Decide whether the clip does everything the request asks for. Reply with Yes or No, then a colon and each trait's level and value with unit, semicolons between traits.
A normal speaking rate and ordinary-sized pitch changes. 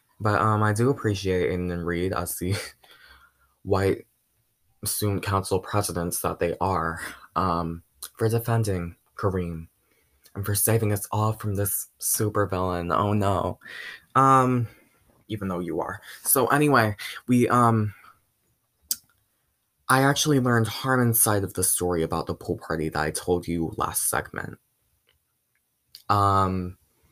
No: slow, 130 wpm; average, 4.2 semitones